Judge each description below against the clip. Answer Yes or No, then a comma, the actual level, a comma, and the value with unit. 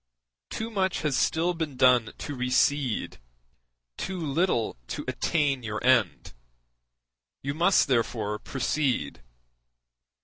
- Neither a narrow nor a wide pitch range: Yes, average, 4.8 semitones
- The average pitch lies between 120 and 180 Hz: Yes, low, 135 Hz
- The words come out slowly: Yes, slow, 105 wpm